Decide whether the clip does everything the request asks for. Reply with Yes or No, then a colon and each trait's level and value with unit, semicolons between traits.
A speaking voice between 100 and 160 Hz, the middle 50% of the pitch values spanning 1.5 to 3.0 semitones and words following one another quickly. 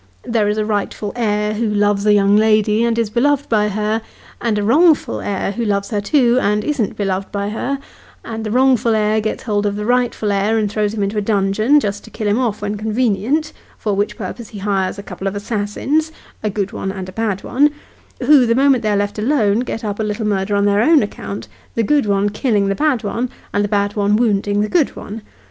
No: high, 210 Hz; narrow, 2.4 semitones; fast, 230 wpm